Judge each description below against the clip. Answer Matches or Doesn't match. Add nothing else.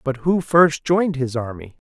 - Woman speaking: Doesn't match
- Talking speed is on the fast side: Doesn't match